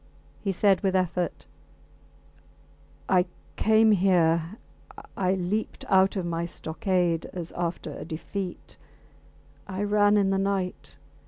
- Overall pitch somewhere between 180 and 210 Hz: Yes, medium, 185 Hz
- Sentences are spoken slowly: Yes, slow, 115 wpm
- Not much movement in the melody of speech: Yes, narrow, 2.3 semitones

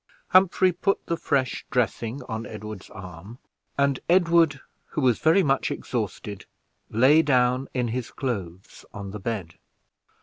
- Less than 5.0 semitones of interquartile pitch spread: No, wide, 5.4 semitones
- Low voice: Yes, low, 125 Hz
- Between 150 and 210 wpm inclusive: No, slow, 135 wpm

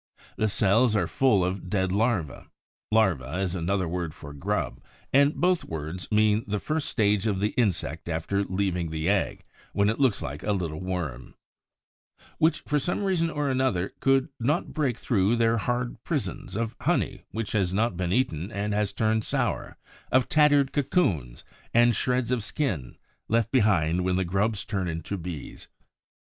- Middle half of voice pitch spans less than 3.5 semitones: No, average, 5.2 semitones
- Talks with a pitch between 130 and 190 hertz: No, low, 105 Hz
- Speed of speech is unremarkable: Yes, average, 165 wpm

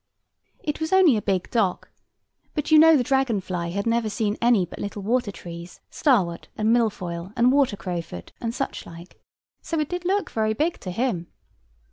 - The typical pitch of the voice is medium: No, high, 220 Hz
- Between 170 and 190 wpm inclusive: Yes, average, 185 wpm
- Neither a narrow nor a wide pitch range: No, wide, 6.8 semitones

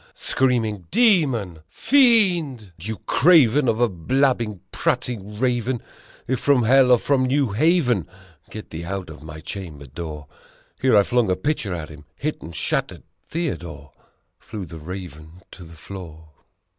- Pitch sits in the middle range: No, low, 110 Hz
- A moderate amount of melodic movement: No, wide, 7.6 semitones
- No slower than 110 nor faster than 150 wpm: Yes, average, 145 wpm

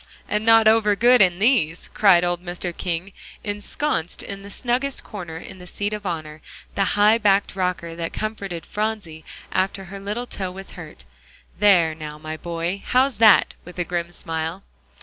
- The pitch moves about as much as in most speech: Yes, average, 3.6 semitones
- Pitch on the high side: Yes, high, 195 Hz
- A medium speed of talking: Yes, average, 170 wpm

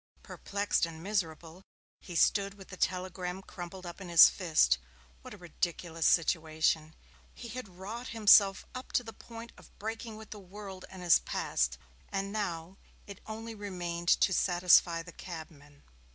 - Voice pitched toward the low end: No, medium, 185 Hz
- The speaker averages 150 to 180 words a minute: Yes, average, 155 wpm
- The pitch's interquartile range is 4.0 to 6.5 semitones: No, average, 3.5 semitones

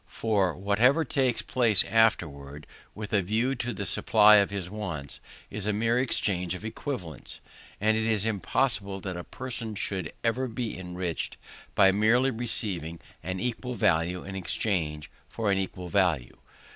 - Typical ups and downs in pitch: Yes, average, 3.9 semitones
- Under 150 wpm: No, average, 155 wpm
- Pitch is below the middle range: Yes, low, 100 Hz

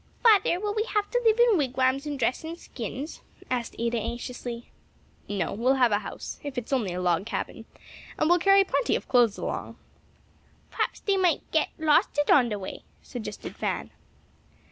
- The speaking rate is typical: Yes, average, 180 wpm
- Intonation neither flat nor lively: No, wide, 7.2 semitones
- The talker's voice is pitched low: No, very high, 265 Hz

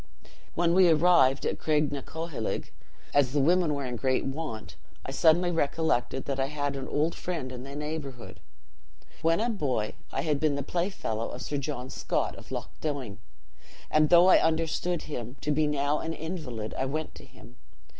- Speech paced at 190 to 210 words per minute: No, average, 175 wpm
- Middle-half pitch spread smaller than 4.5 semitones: Yes, average, 3.5 semitones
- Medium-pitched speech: Yes, medium, 145 Hz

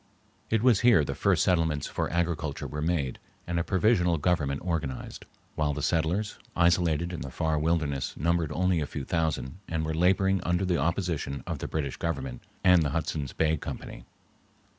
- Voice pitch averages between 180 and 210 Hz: No, very low, 80 Hz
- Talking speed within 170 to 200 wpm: Yes, average, 175 wpm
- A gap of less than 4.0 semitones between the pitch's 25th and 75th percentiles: Yes, average, 3.0 semitones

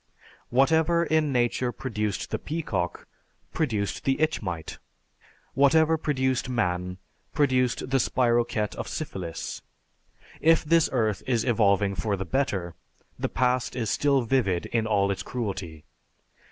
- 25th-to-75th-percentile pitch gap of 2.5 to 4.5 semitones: No, wide, 5.5 semitones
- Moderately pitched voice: No, low, 120 Hz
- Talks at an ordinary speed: No, slow, 125 wpm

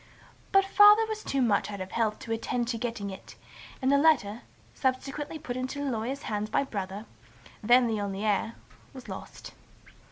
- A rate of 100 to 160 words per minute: No, average, 185 wpm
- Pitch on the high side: Yes, high, 240 Hz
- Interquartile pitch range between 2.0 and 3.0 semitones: No, average, 4.7 semitones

